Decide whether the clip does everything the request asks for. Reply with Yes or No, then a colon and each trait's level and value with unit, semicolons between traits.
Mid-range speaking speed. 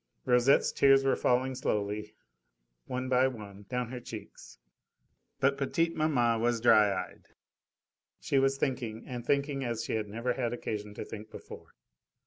Yes: average, 150 wpm